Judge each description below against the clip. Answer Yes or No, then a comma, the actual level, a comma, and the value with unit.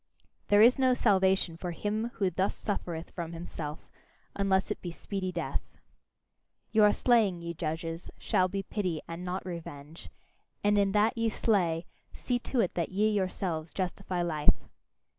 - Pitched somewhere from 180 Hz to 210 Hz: Yes, medium, 185 Hz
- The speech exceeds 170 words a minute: No, average, 155 wpm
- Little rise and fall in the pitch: No, average, 3.5 semitones